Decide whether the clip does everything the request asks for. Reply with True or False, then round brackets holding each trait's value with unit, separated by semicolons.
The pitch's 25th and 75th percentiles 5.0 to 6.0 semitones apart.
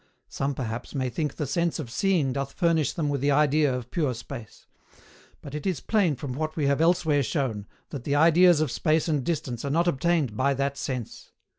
False (3.5 semitones)